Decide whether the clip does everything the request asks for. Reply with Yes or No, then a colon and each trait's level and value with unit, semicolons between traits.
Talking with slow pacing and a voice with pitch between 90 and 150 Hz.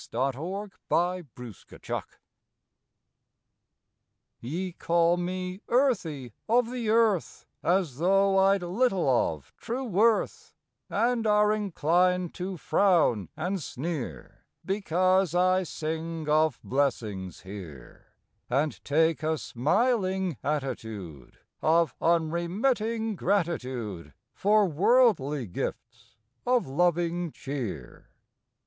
No: slow, 100 wpm; medium, 175 Hz